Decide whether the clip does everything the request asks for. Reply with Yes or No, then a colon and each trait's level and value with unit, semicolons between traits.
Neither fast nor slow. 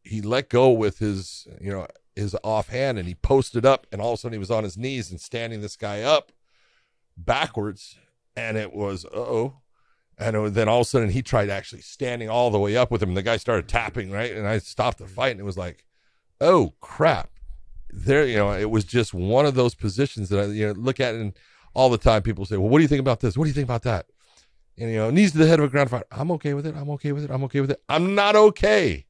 No: fast, 265 wpm